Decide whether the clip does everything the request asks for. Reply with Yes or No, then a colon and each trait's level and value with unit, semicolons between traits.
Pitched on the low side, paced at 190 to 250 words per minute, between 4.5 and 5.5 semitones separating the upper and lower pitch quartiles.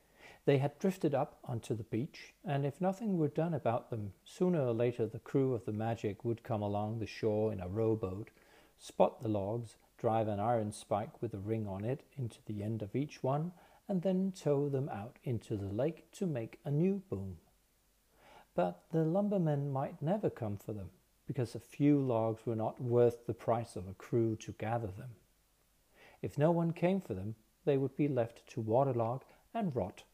Yes: low, 120 Hz; average, 195 wpm; average, 5.2 semitones